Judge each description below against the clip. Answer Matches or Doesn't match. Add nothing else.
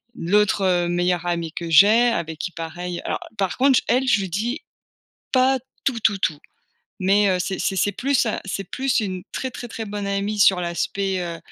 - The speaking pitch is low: Doesn't match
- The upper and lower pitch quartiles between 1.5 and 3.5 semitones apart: Doesn't match